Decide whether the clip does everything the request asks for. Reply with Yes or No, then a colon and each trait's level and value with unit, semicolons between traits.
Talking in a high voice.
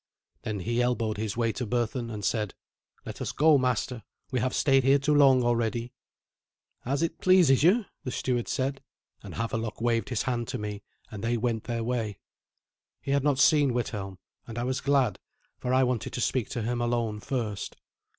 No: low, 120 Hz